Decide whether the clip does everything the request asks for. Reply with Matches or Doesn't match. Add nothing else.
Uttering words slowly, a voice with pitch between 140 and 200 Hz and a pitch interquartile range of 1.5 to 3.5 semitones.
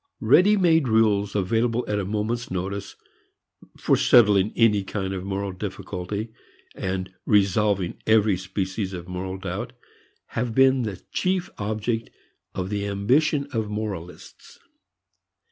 Doesn't match